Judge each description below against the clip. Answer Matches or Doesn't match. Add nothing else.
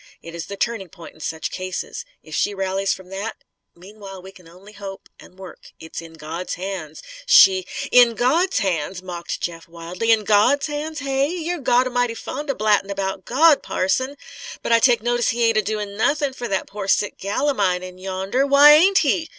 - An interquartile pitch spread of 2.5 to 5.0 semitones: Doesn't match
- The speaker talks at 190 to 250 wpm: Matches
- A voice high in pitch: Matches